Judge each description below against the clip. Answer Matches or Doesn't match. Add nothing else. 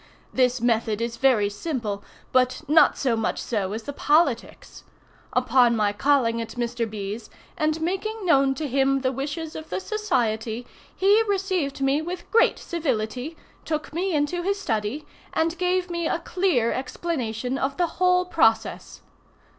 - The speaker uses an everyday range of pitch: Doesn't match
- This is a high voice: Matches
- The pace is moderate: Matches